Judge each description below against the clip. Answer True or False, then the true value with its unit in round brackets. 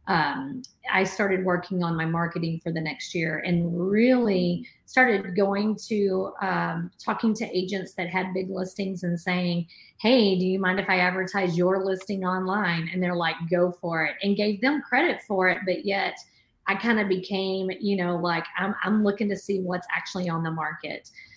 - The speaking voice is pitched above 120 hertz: True (185 Hz)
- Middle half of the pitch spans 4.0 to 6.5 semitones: False (2.4 semitones)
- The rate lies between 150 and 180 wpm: False (190 wpm)